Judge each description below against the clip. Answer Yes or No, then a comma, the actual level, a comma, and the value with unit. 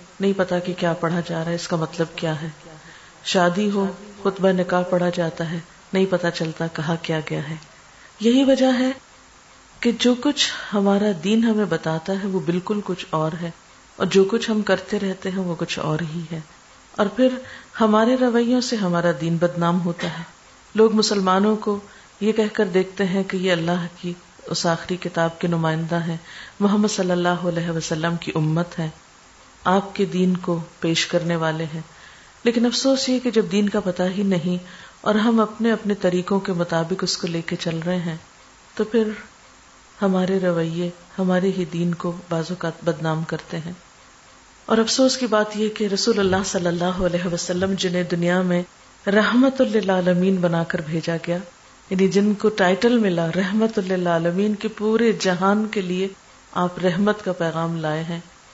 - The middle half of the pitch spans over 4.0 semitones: No, average, 3.5 semitones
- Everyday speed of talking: Yes, average, 180 wpm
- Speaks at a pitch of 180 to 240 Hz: Yes, medium, 185 Hz